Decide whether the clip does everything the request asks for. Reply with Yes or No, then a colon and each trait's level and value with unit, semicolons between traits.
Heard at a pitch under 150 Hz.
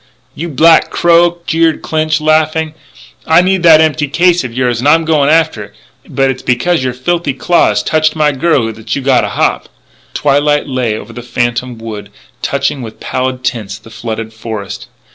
Yes: medium, 140 Hz